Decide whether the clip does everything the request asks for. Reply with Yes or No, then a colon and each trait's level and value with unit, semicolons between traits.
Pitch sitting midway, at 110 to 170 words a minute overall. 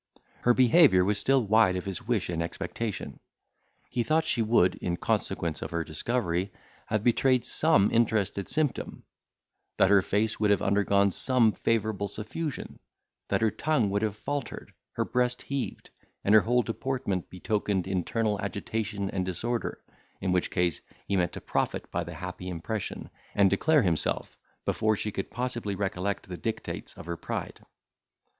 No: low, 105 Hz; average, 160 wpm